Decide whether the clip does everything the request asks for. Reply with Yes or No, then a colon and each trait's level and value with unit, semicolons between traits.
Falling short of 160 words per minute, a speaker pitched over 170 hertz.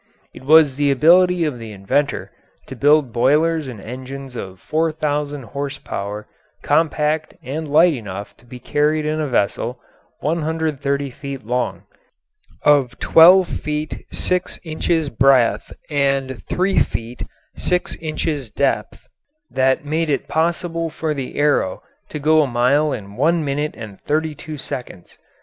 No: average, 140 wpm; medium, 145 Hz